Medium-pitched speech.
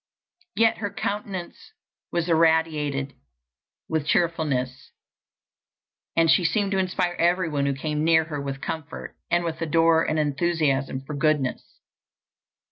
Yes: medium, 160 Hz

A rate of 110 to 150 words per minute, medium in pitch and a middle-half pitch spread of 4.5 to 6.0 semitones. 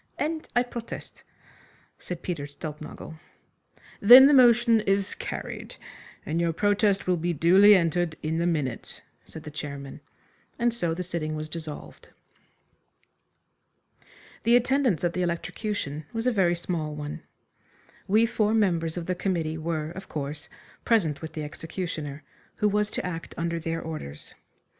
Yes: average, 145 wpm; medium, 170 Hz; average, 4.8 semitones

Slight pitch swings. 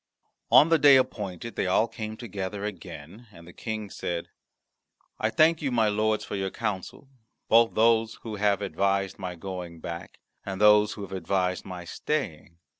No: average, 3.2 semitones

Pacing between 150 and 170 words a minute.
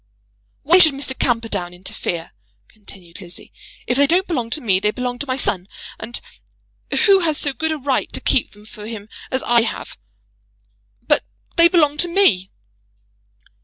Yes: average, 165 wpm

